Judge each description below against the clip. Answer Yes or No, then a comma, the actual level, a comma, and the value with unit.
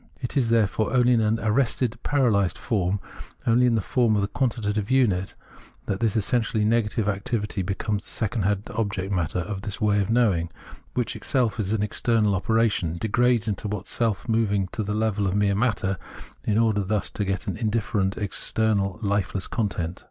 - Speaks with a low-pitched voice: Yes, low, 105 Hz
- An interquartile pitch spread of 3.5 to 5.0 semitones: No, narrow, 2.5 semitones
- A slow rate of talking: No, average, 175 wpm